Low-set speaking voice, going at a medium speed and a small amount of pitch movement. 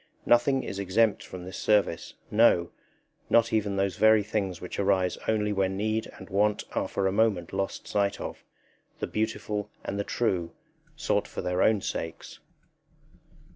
Yes: low, 100 Hz; average, 160 wpm; narrow, 2.3 semitones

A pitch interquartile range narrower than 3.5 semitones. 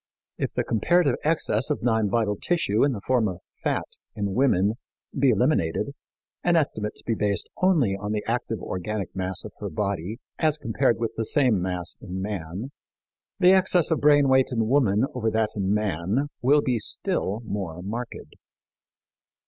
No: average, 5.0 semitones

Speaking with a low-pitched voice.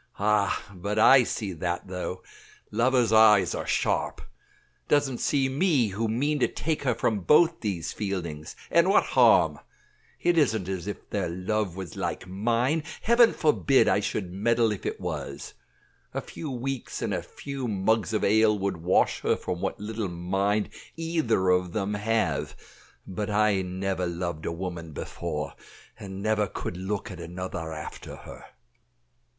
Yes: low, 105 Hz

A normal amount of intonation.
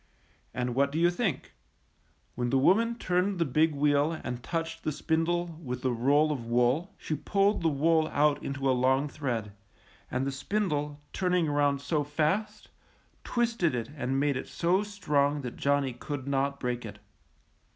Yes: average, 4.0 semitones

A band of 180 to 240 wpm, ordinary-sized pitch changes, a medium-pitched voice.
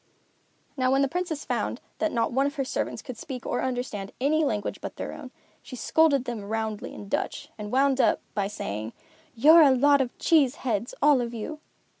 No: average, 200 wpm; average, 4.2 semitones; very high, 255 Hz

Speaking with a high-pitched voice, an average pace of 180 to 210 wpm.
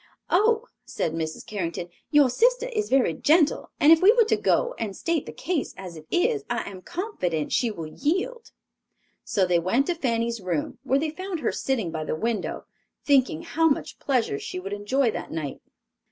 Yes: very high, 260 Hz; average, 190 wpm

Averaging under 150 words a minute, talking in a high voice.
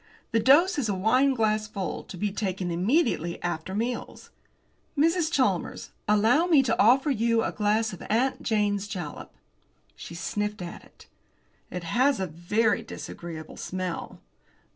Yes: average, 140 wpm; high, 215 Hz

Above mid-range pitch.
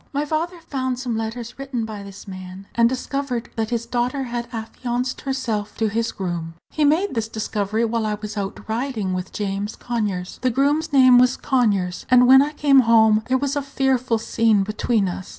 Yes: high, 235 Hz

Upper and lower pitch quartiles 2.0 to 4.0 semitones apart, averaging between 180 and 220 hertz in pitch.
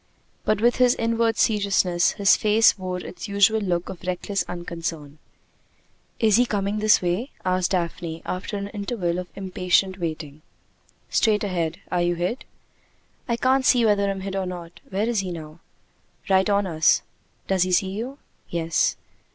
Yes: average, 3.3 semitones; high, 190 Hz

